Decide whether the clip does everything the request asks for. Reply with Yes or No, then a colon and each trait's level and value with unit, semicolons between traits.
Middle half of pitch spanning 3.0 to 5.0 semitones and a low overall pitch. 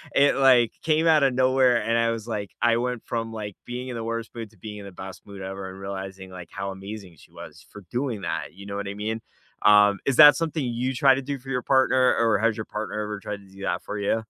Yes: average, 4.0 semitones; low, 110 Hz